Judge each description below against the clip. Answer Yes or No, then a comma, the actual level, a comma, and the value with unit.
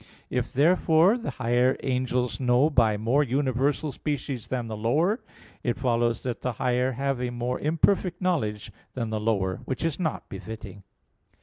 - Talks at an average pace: Yes, average, 160 wpm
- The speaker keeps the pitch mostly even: No, average, 3.9 semitones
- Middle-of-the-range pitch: No, low, 125 Hz